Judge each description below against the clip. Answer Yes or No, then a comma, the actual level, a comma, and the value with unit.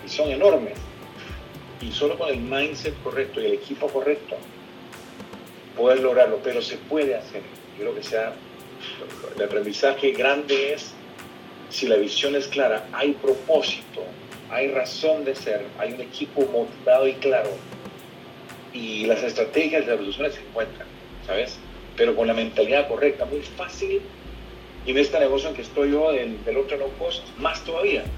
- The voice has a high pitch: No, medium, 140 Hz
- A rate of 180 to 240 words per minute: No, average, 160 wpm